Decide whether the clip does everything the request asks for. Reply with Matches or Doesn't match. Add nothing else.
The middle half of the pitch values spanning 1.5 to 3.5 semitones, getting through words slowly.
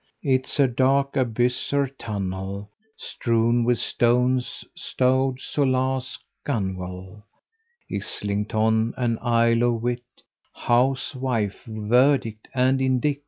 Matches